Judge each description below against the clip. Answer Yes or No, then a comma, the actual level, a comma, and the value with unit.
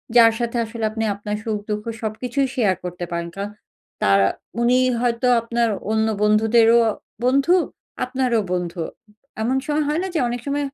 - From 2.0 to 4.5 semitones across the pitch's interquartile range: Yes, average, 2.9 semitones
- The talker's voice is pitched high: Yes, high, 225 Hz